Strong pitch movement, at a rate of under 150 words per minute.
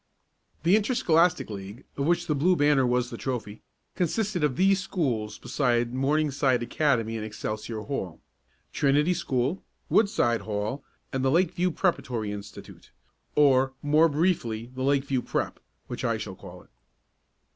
Yes: wide, 5.8 semitones; average, 140 wpm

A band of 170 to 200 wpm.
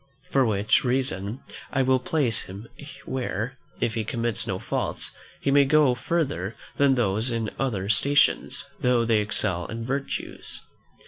No: average, 145 wpm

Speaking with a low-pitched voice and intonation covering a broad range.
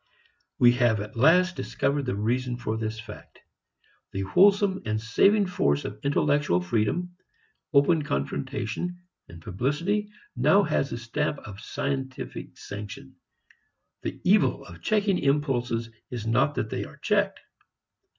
Yes: low, 125 Hz; wide, 6.1 semitones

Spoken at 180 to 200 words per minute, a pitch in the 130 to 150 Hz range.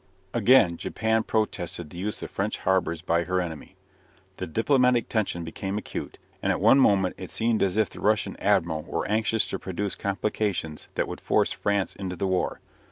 No: average, 185 wpm; very low, 95 Hz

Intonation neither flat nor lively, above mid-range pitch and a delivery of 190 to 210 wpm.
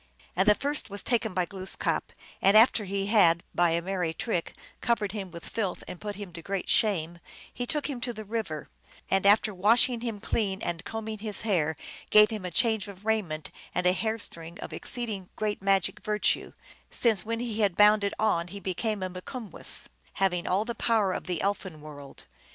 Yes: average, 3.4 semitones; high, 200 Hz; average, 195 wpm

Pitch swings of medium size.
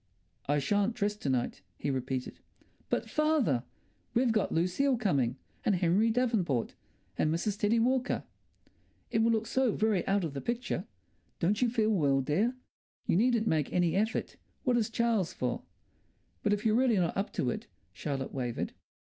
No: wide, 6.8 semitones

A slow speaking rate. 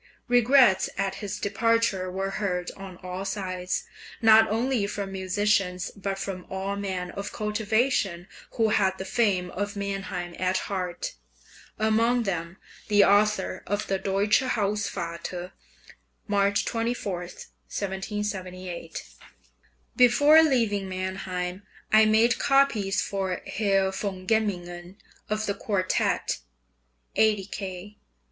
Yes: slow, 110 wpm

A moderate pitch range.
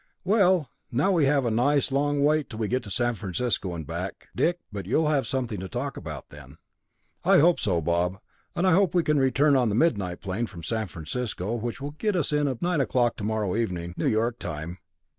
No: wide, 6.9 semitones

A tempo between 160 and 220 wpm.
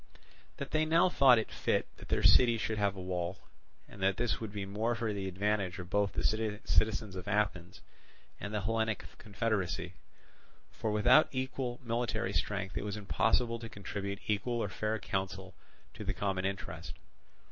Yes: average, 170 wpm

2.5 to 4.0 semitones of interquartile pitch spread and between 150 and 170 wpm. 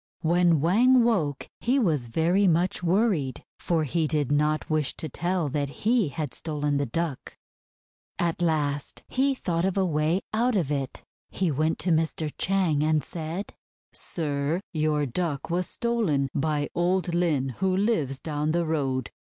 Yes: average, 3.7 semitones; average, 160 wpm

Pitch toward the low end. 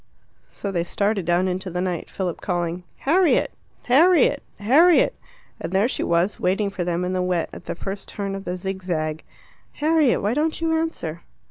No: high, 190 Hz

